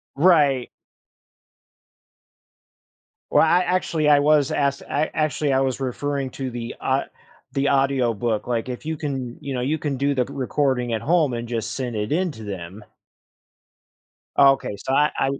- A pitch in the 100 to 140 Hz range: Yes, low, 135 Hz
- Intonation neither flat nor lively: Yes, average, 3.1 semitones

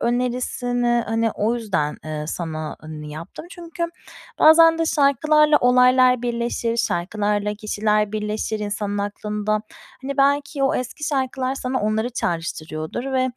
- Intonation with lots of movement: No, average, 4.0 semitones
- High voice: Yes, high, 235 Hz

